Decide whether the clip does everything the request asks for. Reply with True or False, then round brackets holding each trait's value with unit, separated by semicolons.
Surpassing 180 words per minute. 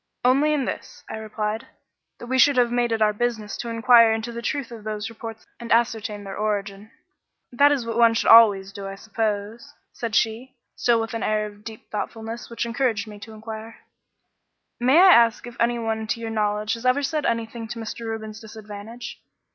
True (195 wpm)